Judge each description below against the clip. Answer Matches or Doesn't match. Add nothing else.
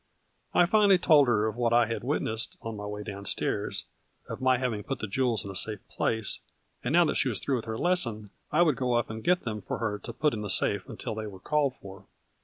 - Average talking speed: Doesn't match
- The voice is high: Doesn't match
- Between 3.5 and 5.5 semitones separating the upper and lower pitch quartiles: Matches